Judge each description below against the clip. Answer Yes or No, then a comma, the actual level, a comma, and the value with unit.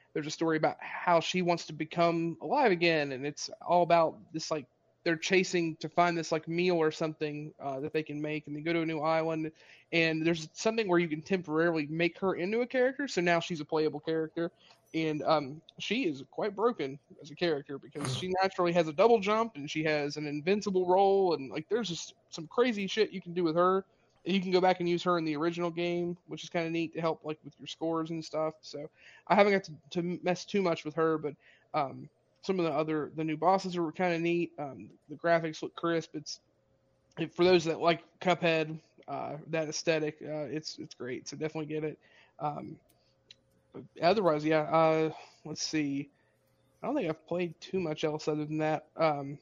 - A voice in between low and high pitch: Yes, medium, 165 Hz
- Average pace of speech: No, fast, 220 wpm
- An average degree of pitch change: No, narrow, 2.2 semitones